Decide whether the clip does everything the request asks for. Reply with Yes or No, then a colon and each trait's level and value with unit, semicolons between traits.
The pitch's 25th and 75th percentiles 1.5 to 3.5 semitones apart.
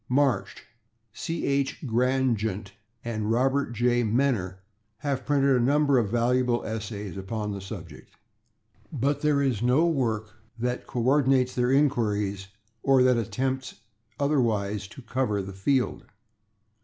No: average, 4.0 semitones